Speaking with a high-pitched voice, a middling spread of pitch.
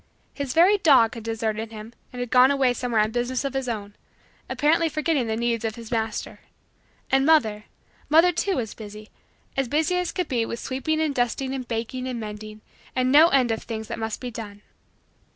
Yes: high, 245 Hz; average, 3.8 semitones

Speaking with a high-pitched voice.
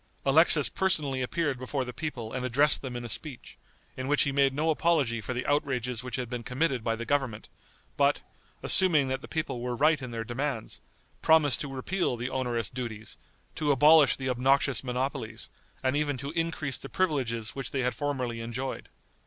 No: low, 130 Hz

